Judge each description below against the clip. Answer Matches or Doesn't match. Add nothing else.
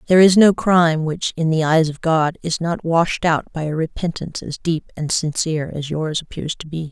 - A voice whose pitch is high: Doesn't match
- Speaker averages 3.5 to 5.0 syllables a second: Doesn't match